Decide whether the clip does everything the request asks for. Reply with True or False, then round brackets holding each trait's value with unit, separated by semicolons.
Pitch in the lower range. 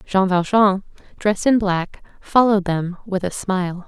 False (195 Hz)